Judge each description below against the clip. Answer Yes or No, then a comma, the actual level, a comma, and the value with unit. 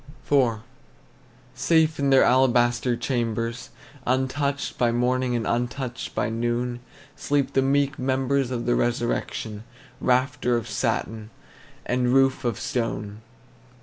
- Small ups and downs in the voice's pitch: Yes, narrow, 2.0 semitones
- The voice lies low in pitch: Yes, low, 125 Hz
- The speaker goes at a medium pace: No, slow, 115 wpm